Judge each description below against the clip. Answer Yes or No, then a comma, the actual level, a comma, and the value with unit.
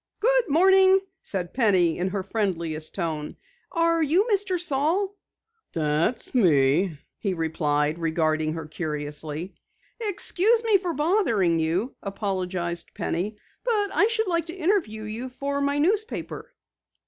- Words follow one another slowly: Yes, slow, 125 wpm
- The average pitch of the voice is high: Yes, high, 215 Hz